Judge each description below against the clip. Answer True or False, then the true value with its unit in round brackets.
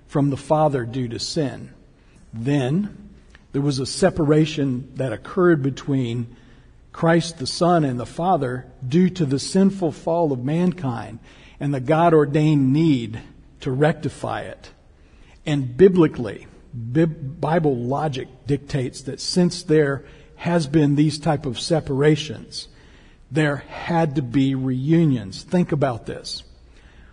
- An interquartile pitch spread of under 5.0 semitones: True (3.8 semitones)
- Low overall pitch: False (145 Hz)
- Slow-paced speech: True (125 wpm)